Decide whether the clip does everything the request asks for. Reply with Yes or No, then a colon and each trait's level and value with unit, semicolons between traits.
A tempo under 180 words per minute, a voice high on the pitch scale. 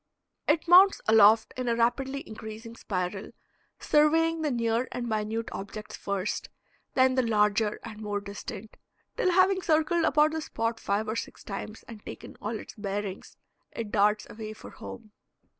Yes: average, 160 wpm; high, 225 Hz